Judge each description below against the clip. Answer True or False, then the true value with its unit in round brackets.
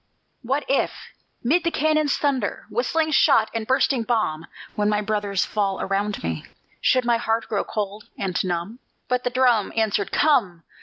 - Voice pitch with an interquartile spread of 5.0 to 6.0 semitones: False (4.3 semitones)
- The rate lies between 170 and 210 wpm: False (160 wpm)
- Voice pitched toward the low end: False (225 Hz)